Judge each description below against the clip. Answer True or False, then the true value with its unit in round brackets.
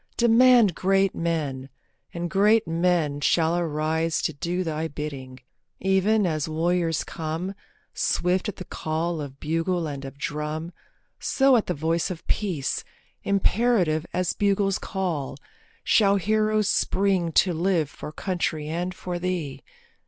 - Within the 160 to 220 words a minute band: False (135 wpm)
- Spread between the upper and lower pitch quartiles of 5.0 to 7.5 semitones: False (3.7 semitones)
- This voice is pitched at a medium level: True (170 Hz)